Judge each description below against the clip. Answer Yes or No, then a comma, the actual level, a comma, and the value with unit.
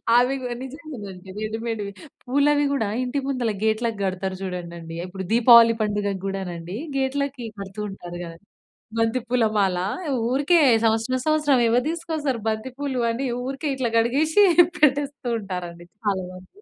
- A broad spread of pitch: Yes, wide, 5.7 semitones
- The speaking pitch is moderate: No, high, 230 Hz